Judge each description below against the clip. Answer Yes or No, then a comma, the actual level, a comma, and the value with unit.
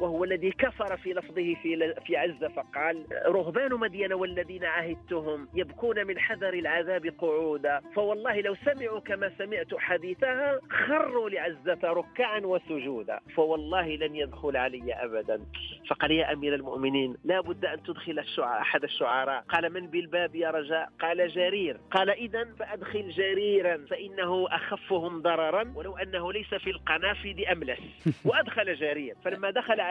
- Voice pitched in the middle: Yes, medium, 180 Hz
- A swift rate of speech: Yes, fast, 140 wpm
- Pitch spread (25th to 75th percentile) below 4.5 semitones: Yes, average, 3.5 semitones